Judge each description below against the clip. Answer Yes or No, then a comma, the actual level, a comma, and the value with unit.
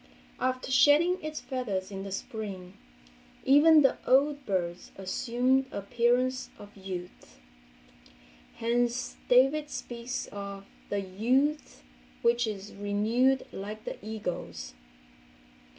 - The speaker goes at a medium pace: No, slow, 105 wpm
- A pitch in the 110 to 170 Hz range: No, high, 235 Hz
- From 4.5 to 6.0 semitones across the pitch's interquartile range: Yes, average, 4.8 semitones